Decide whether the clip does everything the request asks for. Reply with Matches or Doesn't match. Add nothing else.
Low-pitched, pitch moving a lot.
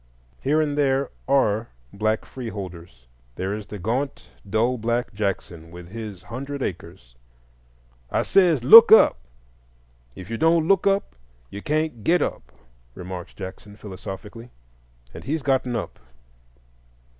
Matches